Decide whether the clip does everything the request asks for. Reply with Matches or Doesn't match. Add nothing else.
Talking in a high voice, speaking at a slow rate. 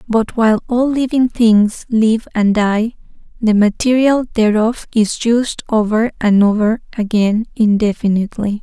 Matches